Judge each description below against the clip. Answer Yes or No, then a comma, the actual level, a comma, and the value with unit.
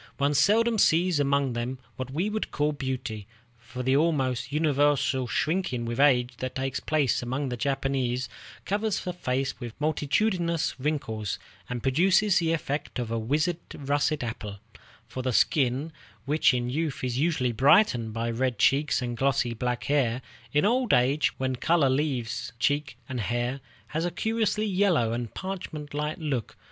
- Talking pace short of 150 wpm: No, average, 160 wpm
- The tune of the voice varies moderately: Yes, average, 4.1 semitones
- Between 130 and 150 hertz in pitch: Yes, medium, 140 Hz